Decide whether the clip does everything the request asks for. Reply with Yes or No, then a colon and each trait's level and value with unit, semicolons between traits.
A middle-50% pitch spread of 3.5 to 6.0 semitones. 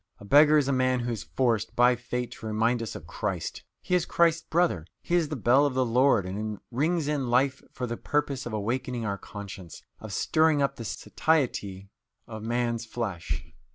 Yes: average, 4.4 semitones